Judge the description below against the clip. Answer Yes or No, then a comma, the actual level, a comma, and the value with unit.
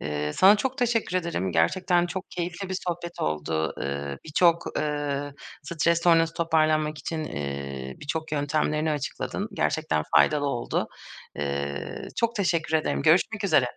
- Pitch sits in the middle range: Yes, medium, 155 Hz